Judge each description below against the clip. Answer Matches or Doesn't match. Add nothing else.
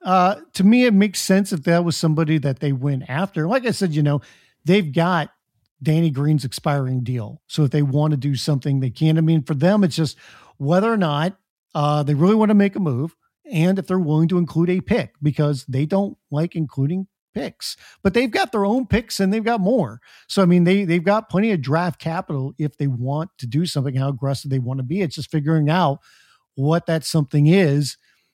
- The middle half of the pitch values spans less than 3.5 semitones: Doesn't match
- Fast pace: Matches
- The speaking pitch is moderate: Matches